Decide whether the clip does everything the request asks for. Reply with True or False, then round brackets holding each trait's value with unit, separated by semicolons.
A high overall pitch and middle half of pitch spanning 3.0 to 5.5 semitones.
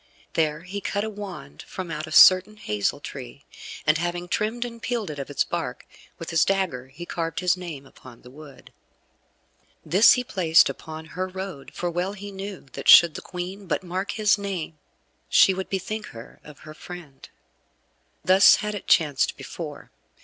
False (175 Hz; 4.2 semitones)